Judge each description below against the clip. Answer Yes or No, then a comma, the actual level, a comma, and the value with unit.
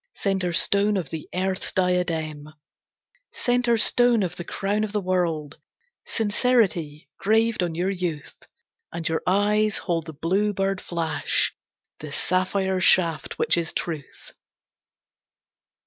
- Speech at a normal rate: No, slow, 125 wpm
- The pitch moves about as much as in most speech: Yes, average, 3.7 semitones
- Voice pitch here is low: No, medium, 185 Hz